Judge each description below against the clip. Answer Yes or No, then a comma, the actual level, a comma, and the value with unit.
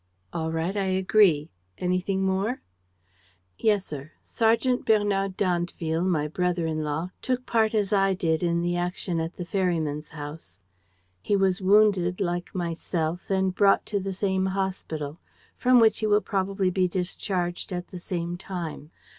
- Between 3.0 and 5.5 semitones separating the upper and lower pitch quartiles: No, narrow, 2.6 semitones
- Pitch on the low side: No, medium, 185 Hz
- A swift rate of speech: No, average, 155 wpm